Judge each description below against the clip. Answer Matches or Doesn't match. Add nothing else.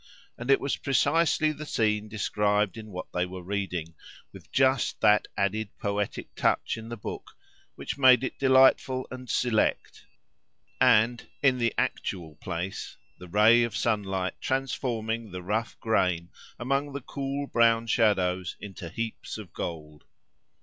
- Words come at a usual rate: Matches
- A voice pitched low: Matches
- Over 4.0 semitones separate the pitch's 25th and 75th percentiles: Matches